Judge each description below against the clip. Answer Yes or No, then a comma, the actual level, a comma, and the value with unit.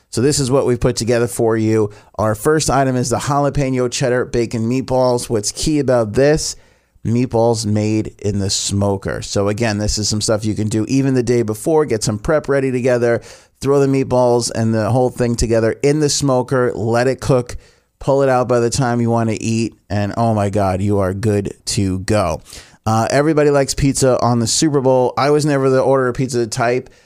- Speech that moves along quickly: Yes, fast, 210 wpm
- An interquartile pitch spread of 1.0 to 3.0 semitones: No, average, 3.4 semitones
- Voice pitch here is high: No, low, 120 Hz